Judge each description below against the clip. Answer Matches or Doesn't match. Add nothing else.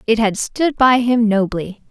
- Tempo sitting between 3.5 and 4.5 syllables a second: Matches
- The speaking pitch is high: Matches